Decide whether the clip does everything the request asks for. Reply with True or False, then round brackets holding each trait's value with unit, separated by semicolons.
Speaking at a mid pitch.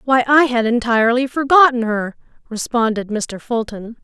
False (240 Hz)